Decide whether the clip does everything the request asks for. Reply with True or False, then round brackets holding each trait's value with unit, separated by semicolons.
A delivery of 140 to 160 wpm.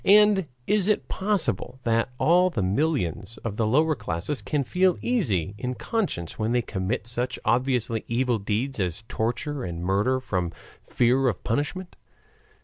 True (150 wpm)